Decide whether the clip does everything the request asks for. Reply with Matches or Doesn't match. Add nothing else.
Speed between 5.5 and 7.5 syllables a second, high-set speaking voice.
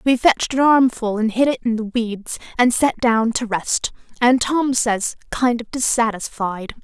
Doesn't match